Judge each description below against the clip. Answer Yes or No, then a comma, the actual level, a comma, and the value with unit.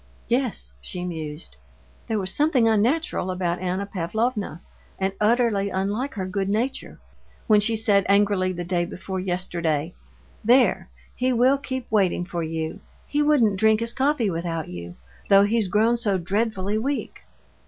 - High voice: Yes, high, 200 Hz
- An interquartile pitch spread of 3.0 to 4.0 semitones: No, average, 4.4 semitones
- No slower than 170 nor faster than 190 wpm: No, average, 150 wpm